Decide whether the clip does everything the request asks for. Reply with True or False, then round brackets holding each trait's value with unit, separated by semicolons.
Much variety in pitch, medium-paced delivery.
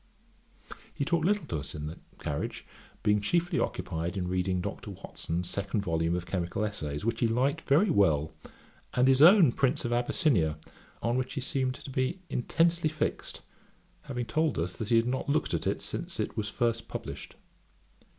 True (7.8 semitones; 180 wpm)